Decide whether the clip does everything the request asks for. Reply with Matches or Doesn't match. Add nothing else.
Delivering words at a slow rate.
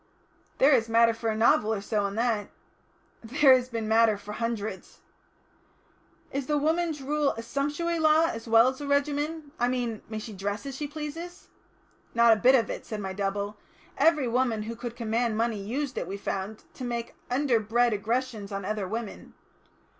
Doesn't match